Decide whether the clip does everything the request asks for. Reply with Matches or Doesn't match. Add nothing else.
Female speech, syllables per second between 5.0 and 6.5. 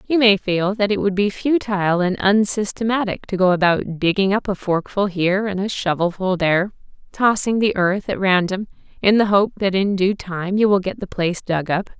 Matches